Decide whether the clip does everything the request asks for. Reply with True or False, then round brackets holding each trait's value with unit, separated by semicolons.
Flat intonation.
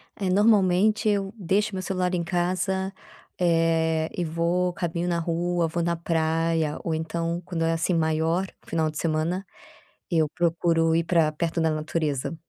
True (1.9 semitones)